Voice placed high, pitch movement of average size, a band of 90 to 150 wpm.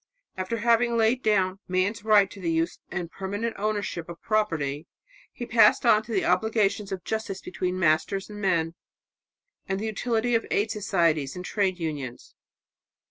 No: high, 195 Hz; average, 3.8 semitones; average, 160 wpm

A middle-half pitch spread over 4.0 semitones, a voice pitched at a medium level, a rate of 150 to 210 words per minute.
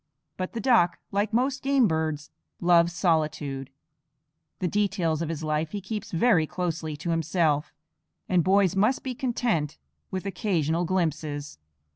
No: average, 4.4 semitones; medium, 175 Hz; average, 140 wpm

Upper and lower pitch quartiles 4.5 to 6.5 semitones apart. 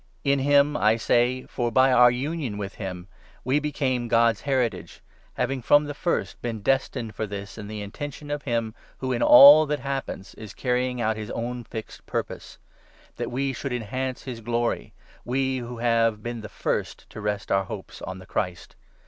No: average, 3.5 semitones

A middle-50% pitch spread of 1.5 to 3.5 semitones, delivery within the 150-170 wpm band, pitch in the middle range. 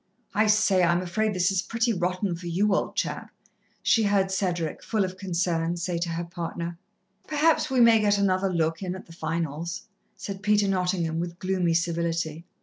No: average, 2.8 semitones; average, 180 wpm; medium, 180 Hz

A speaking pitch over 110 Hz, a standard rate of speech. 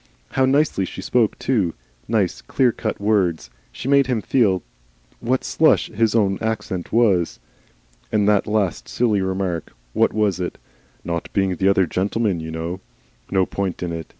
No: low, 100 Hz; average, 160 wpm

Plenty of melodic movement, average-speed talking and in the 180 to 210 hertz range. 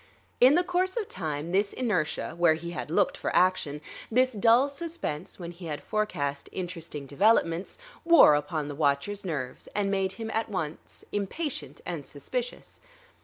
Yes: wide, 6.8 semitones; average, 160 wpm; medium, 185 Hz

